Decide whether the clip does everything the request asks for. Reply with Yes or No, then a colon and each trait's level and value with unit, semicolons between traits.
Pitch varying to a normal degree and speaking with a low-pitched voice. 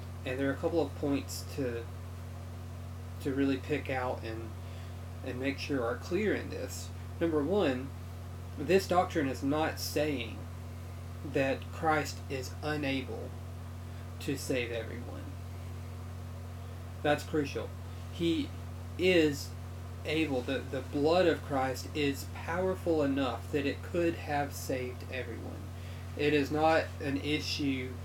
No: wide, 6.3 semitones; very low, 90 Hz